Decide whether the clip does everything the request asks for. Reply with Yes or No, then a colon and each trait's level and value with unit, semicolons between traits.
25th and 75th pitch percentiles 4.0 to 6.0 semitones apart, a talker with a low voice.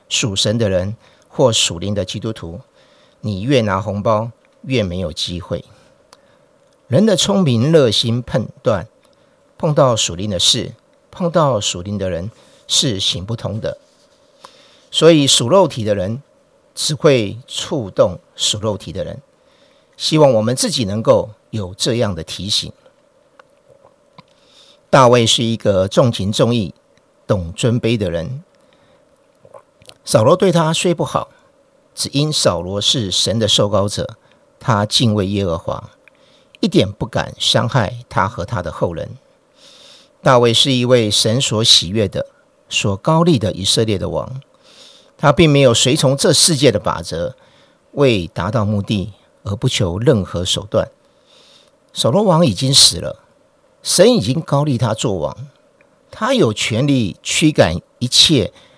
Yes: wide, 5.4 semitones; low, 115 Hz